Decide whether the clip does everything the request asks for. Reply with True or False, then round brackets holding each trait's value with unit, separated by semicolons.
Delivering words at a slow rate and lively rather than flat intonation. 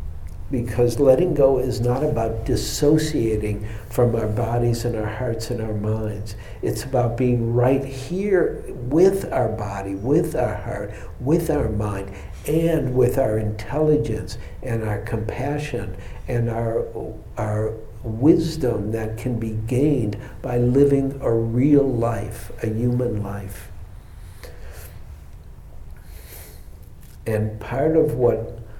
False (120 wpm; 3.5 semitones)